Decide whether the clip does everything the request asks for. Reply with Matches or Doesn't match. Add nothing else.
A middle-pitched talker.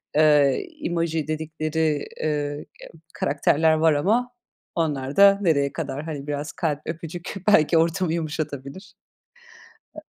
Matches